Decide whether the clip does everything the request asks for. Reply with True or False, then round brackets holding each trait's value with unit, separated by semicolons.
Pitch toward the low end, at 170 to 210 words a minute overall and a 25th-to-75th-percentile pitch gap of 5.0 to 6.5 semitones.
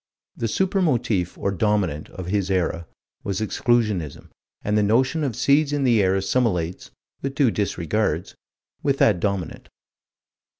False (105 Hz; 140 wpm; 5.4 semitones)